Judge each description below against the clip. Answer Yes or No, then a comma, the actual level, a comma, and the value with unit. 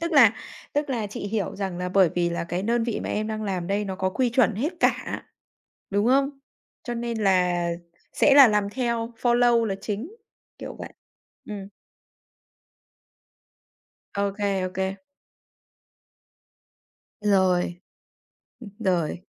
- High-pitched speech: Yes, high, 205 Hz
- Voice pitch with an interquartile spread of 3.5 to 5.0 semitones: Yes, average, 3.9 semitones